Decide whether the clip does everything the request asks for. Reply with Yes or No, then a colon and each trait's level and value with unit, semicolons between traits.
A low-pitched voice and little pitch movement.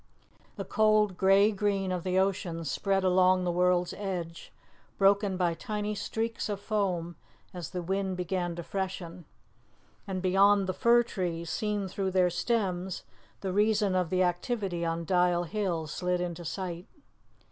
No: medium, 185 Hz; narrow, 2.3 semitones